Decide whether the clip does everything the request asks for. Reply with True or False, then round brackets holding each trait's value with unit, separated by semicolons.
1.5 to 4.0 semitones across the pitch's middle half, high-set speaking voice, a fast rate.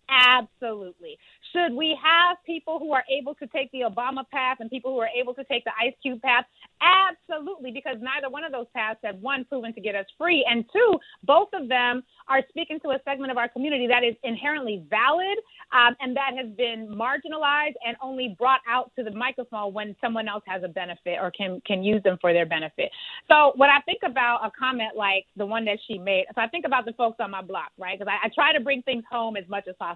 False (4.5 semitones; 250 Hz; 235 wpm)